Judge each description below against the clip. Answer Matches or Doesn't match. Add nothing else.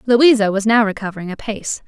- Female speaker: Matches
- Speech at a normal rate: Matches